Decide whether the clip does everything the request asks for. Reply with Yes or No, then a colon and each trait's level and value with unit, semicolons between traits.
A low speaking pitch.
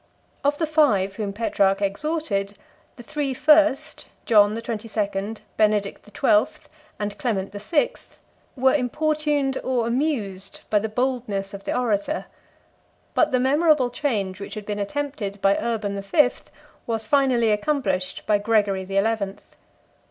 No: high, 220 Hz